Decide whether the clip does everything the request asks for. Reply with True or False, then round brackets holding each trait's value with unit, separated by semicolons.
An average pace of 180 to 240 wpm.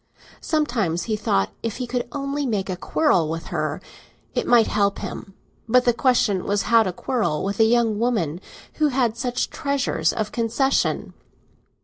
False (170 wpm)